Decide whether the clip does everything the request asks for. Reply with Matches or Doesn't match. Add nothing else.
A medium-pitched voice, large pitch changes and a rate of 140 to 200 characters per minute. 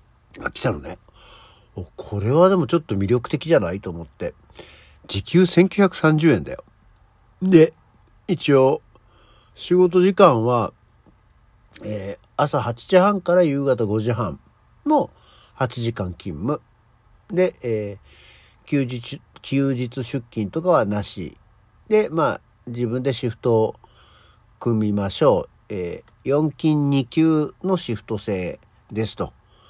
Doesn't match